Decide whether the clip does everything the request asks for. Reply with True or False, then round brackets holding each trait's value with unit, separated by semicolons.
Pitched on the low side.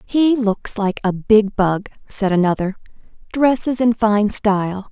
False (210 Hz)